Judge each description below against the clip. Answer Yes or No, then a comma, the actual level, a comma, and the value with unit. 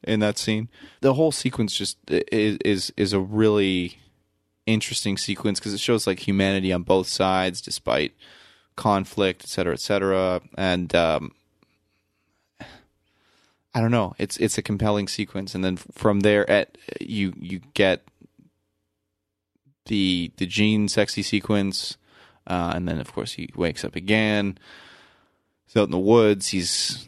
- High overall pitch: No, low, 100 Hz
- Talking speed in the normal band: Yes, average, 145 wpm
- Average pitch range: No, narrow, 2.1 semitones